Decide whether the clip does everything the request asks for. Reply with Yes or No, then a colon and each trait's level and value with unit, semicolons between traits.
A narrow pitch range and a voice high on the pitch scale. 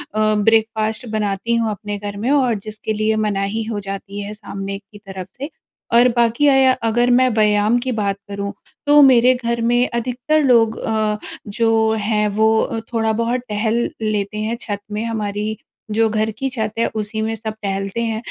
Yes: narrow, 2.1 semitones; high, 220 Hz